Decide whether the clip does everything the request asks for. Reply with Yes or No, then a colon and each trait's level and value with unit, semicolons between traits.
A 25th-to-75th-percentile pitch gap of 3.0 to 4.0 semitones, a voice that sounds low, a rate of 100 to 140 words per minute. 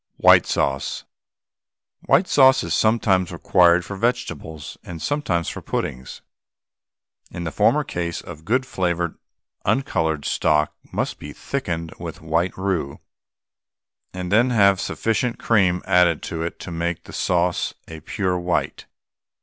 Yes: average, 3.5 semitones; very low, 90 Hz; slow, 135 wpm